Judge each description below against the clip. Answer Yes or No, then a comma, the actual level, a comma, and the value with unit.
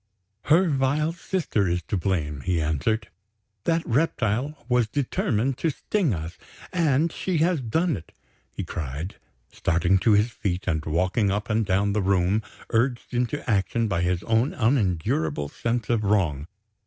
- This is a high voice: No, low, 110 Hz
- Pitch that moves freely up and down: Yes, wide, 7.0 semitones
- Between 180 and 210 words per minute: No, average, 155 wpm